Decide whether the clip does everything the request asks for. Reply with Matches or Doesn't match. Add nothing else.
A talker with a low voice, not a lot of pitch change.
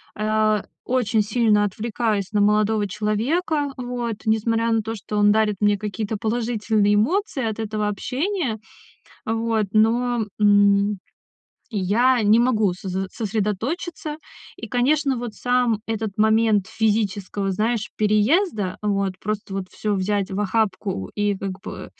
Doesn't match